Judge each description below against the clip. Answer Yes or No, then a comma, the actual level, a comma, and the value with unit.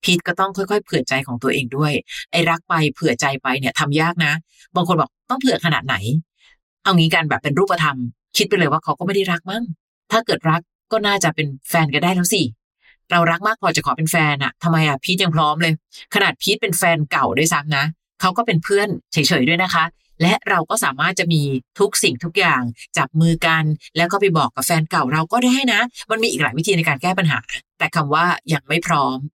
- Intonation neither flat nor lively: Yes, average, 3.9 semitones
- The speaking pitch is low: No, medium, 170 Hz